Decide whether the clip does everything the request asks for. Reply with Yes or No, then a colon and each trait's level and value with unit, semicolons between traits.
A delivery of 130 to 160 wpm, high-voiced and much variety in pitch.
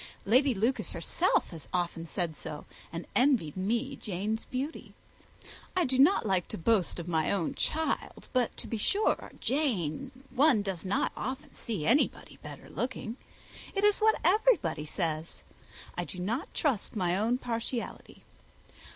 Yes: average, 150 wpm; high, 225 Hz; wide, 7.2 semitones